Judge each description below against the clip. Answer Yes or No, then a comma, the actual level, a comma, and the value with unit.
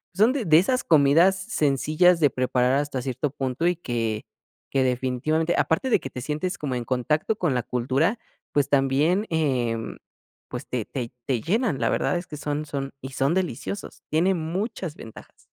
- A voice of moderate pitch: Yes, medium, 145 Hz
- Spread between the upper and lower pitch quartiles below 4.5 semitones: No, average, 5.2 semitones